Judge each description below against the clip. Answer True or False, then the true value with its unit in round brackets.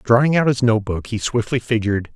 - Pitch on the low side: True (115 Hz)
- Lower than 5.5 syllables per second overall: False (5.9 syllables/s)